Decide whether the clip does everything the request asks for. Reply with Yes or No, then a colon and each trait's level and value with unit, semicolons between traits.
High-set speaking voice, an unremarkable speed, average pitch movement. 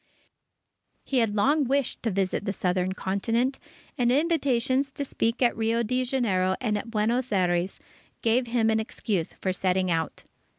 Yes: high, 225 Hz; average, 155 wpm; average, 4.9 semitones